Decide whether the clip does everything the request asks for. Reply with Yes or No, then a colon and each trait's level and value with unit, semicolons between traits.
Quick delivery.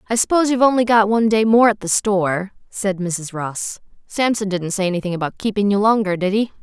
Yes: fast, 215 wpm